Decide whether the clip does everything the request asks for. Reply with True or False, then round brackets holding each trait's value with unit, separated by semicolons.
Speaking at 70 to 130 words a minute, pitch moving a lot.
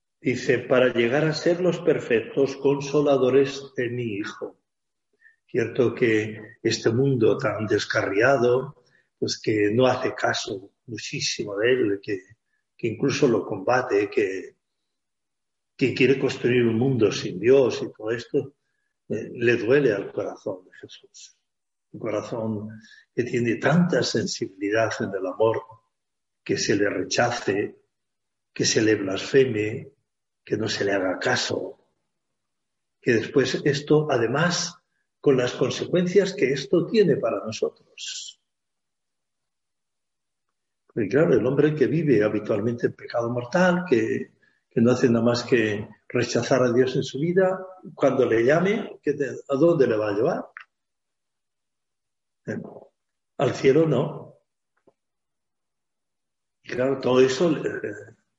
True (125 wpm; 6.7 semitones)